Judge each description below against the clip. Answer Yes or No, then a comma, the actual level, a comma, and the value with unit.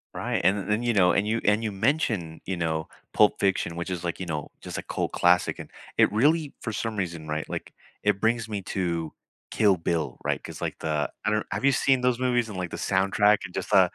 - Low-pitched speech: Yes, low, 100 Hz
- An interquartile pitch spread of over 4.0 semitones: Yes, average, 4.5 semitones